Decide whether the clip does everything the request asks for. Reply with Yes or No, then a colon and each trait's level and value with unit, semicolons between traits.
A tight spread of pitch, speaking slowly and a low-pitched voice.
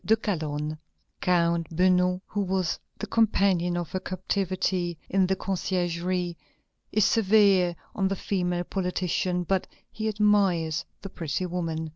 No: narrow, 2.1 semitones; slow, 130 wpm; medium, 180 Hz